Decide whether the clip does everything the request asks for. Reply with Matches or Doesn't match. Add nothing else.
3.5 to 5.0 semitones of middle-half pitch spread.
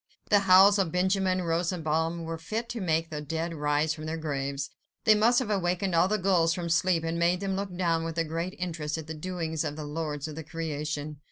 Doesn't match